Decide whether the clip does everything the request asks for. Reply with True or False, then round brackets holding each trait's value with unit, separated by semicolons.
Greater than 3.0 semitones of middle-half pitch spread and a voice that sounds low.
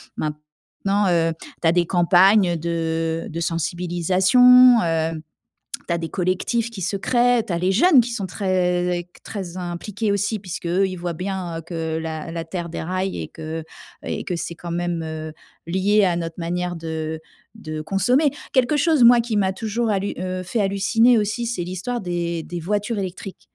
False (3.5 semitones; 180 Hz)